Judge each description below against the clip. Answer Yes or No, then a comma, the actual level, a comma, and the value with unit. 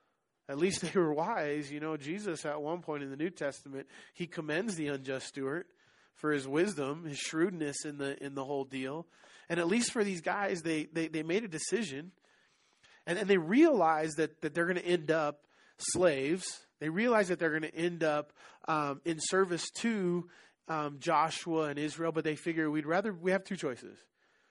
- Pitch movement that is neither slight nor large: Yes, average, 3.1 semitones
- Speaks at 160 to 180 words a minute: No, average, 195 wpm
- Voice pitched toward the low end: No, medium, 160 Hz